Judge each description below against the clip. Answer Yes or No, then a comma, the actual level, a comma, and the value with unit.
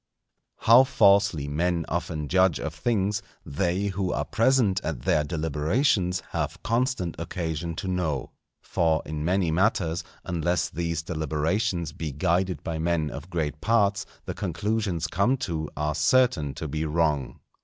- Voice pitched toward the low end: Yes, very low, 85 Hz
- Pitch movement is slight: No, average, 4.1 semitones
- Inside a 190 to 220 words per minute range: No, average, 145 wpm